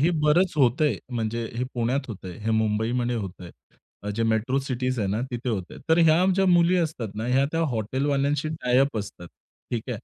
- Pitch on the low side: Yes, low, 125 Hz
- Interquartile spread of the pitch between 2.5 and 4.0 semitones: No, average, 4.8 semitones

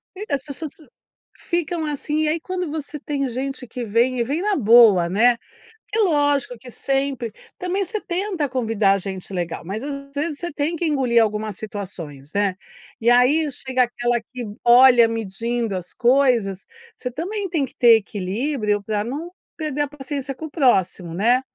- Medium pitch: No, very high, 255 Hz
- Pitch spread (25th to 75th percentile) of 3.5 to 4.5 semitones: No, average, 5.3 semitones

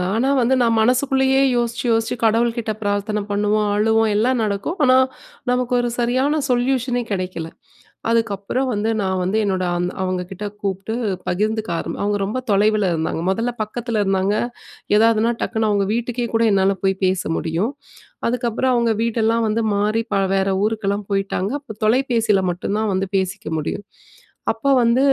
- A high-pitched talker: Yes, high, 220 Hz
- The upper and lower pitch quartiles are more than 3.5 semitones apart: No, average, 3.2 semitones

